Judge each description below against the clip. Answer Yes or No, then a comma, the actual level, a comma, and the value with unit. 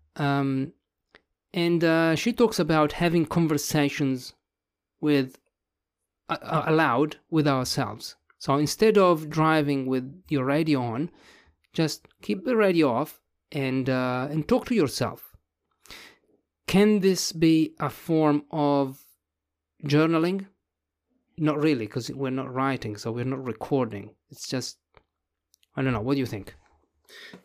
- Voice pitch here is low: No, medium, 145 Hz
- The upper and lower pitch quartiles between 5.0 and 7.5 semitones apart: No, average, 3.9 semitones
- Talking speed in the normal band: No, slow, 130 wpm